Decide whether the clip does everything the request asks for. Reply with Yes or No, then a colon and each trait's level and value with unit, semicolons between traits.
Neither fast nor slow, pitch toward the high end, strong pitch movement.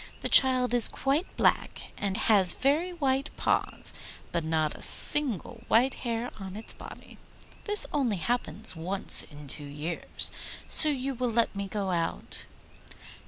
Yes: average, 150 wpm; high, 230 Hz; wide, 6.3 semitones